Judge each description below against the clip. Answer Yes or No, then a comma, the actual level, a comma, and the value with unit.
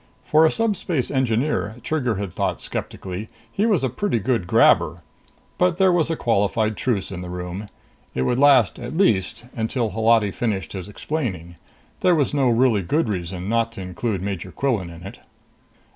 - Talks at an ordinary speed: Yes, average, 175 wpm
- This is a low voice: Yes, low, 115 Hz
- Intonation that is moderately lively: No, wide, 6.5 semitones